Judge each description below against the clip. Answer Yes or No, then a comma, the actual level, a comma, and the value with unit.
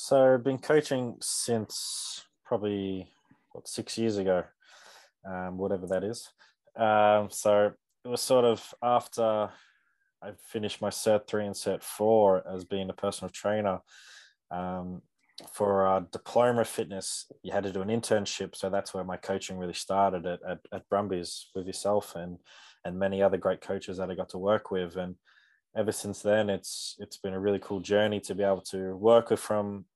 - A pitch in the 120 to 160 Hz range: No, low, 100 Hz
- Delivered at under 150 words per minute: No, average, 180 wpm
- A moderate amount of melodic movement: No, narrow, 2.2 semitones